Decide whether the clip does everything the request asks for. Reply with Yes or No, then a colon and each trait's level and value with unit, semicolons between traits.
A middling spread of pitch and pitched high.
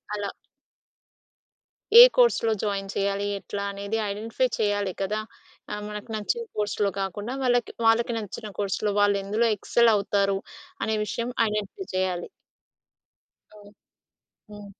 No: narrow, 1.9 semitones; high, 205 Hz